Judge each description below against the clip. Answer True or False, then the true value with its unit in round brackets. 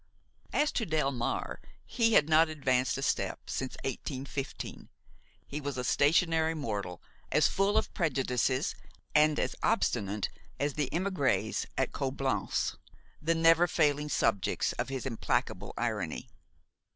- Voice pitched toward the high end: False (145 Hz)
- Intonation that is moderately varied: True (4.2 semitones)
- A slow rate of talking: True (125 wpm)